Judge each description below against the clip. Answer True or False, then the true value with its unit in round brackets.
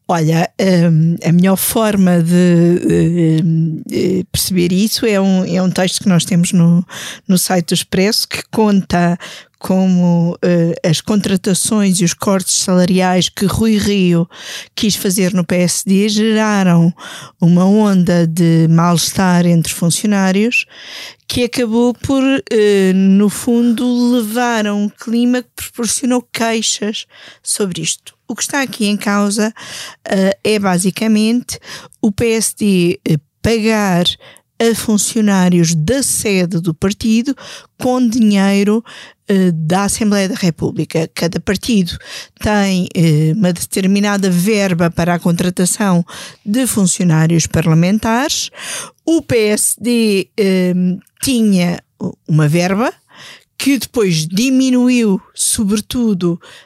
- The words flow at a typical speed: False (110 wpm)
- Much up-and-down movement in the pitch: False (3.9 semitones)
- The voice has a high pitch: True (195 Hz)